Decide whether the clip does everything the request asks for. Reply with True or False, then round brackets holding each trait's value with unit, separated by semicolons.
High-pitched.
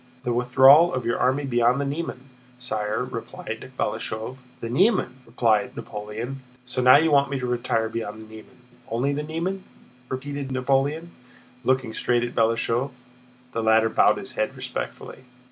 False (125 Hz)